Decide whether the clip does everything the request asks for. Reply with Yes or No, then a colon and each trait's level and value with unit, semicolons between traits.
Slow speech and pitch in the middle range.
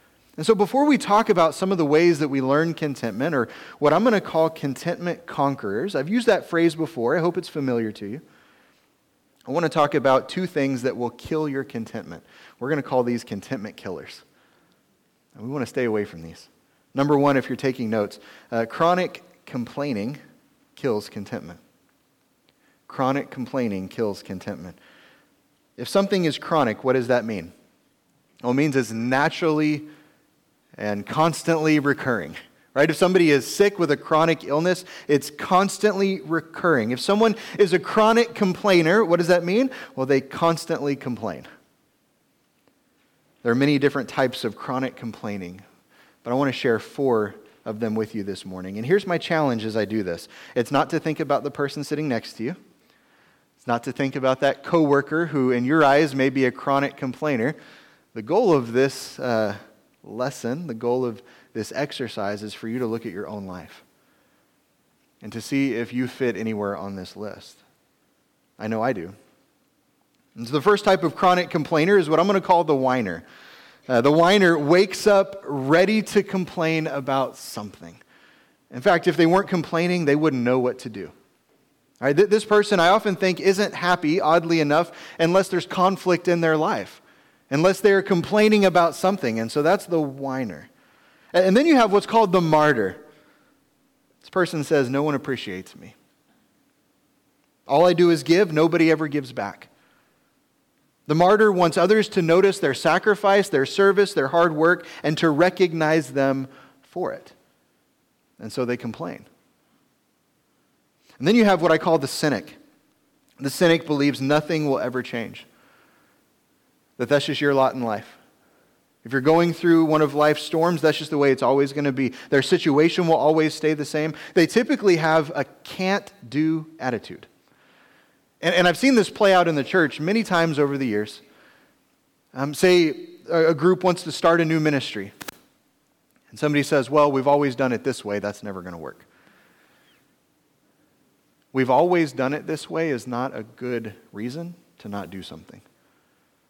No: average, 175 wpm; medium, 150 Hz